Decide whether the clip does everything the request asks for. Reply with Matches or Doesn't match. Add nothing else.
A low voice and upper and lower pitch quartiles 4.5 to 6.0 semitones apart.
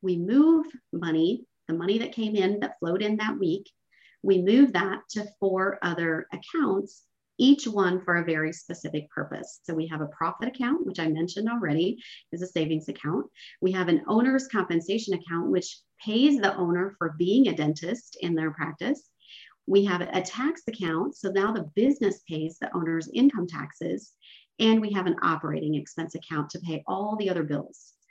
Doesn't match